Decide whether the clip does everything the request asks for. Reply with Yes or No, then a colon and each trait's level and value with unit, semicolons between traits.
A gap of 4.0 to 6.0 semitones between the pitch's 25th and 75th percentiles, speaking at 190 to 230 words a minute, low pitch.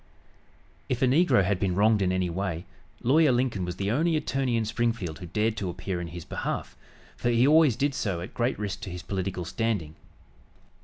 Yes: average, 5.2 semitones; average, 200 wpm; low, 105 Hz